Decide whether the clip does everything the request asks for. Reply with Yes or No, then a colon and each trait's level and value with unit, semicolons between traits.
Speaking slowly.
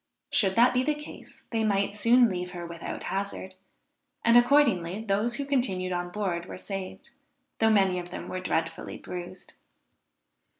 No: average, 160 wpm